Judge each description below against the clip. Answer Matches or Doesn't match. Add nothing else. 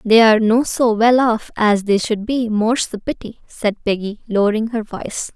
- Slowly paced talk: Doesn't match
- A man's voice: Doesn't match